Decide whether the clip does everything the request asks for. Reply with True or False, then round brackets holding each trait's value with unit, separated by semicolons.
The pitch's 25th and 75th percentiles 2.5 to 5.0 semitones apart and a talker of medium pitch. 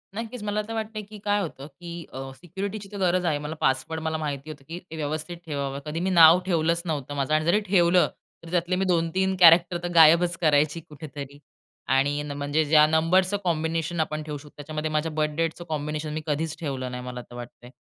True (3.0 semitones; 160 Hz)